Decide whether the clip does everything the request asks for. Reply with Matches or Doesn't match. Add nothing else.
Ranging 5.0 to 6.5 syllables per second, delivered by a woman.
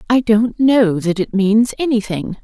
Doesn't match